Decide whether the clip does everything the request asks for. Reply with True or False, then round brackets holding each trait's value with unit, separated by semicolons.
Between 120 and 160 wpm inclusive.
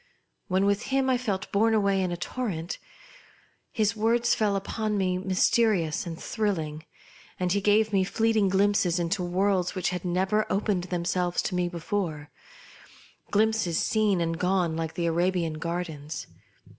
True (150 wpm)